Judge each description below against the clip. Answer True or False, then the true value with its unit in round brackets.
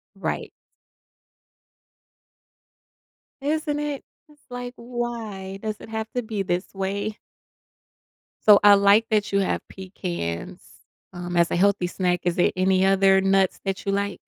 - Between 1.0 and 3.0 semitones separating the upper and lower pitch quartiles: True (2.7 semitones)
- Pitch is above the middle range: True (200 Hz)